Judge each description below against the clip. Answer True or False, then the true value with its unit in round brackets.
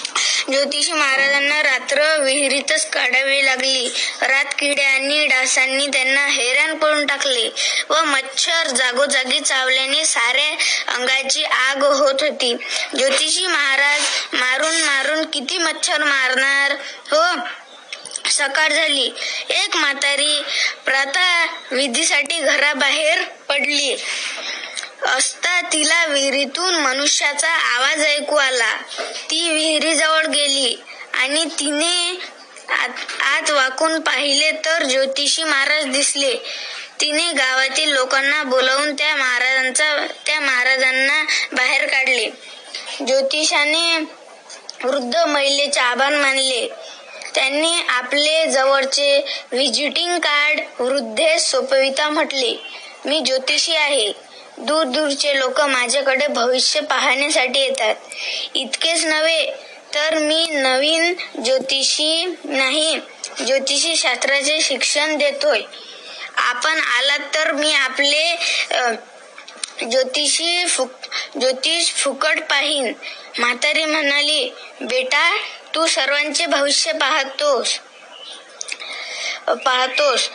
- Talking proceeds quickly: False (85 wpm)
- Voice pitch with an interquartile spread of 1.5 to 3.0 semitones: True (2.6 semitones)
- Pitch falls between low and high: False (290 Hz)